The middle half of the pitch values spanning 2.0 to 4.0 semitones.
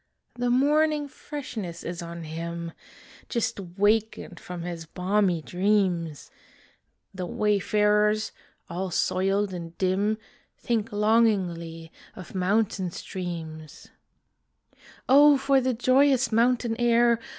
No: average, 5.2 semitones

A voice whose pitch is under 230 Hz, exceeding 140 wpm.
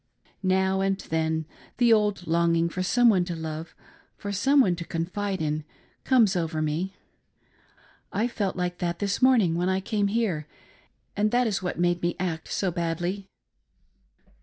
Yes: medium, 185 Hz; average, 160 wpm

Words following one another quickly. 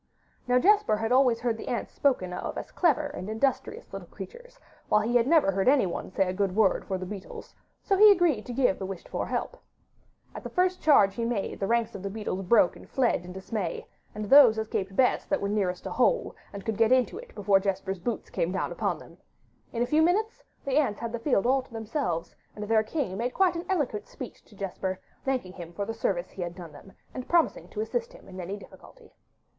Yes: fast, 225 wpm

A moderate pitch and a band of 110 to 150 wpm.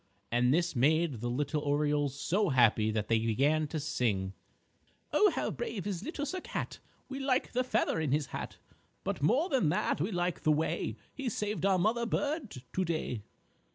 No: medium, 155 Hz; average, 185 wpm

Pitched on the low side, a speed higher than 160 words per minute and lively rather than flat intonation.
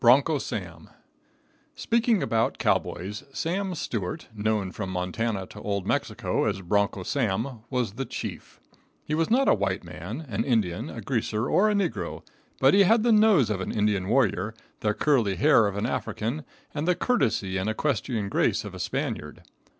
Yes: low, 110 Hz; average, 170 wpm; wide, 7.3 semitones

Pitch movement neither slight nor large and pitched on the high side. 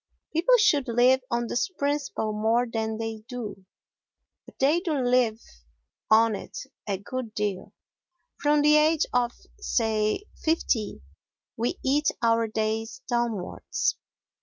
Yes: average, 4.3 semitones; high, 240 Hz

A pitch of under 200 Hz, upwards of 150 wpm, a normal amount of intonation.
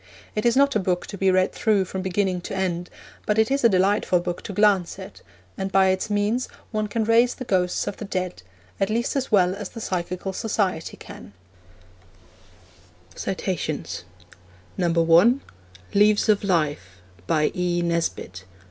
Yes: high, 190 Hz; average, 160 wpm; average, 3.4 semitones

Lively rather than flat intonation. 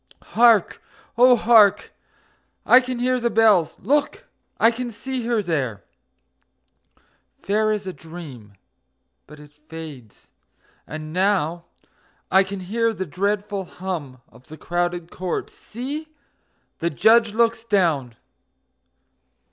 Yes: wide, 6.1 semitones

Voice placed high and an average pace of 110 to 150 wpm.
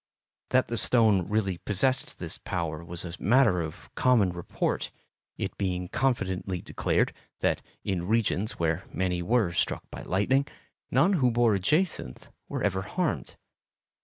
No: low, 100 Hz; average, 145 wpm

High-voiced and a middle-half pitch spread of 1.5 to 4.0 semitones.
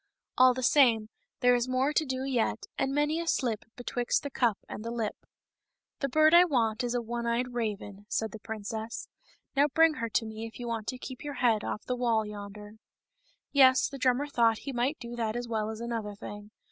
Yes: high, 240 Hz; average, 2.9 semitones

